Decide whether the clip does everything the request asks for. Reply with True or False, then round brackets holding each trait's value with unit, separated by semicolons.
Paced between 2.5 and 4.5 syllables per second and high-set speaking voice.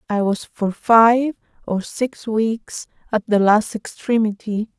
True (3.5 syllables/s; 220 Hz)